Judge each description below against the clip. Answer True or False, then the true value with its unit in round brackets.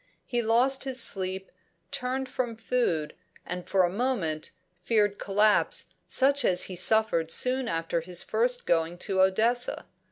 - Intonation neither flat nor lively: False (5.9 semitones)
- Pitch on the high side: True (210 Hz)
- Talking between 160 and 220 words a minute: False (150 wpm)